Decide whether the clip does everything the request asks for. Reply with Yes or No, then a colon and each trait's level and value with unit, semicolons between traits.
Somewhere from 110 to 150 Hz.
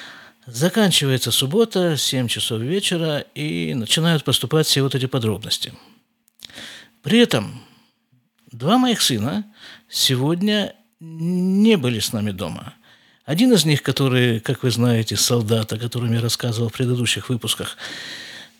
Yes: low, 135 Hz